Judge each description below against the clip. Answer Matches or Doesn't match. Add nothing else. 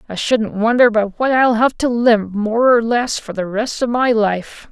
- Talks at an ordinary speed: Doesn't match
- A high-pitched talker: Matches